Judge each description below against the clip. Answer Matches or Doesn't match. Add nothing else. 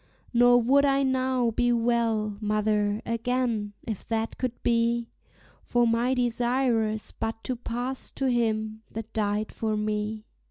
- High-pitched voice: Matches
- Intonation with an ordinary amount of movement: Doesn't match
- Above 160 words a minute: Doesn't match